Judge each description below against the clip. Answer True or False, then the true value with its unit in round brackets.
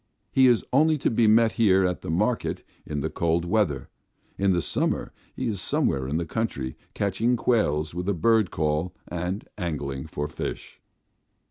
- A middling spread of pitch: False (6.2 semitones)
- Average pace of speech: True (170 wpm)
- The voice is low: True (90 Hz)